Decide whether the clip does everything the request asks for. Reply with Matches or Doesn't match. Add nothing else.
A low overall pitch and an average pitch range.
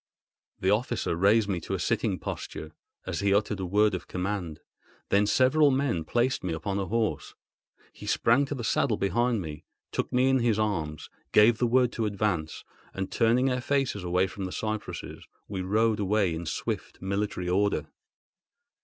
Matches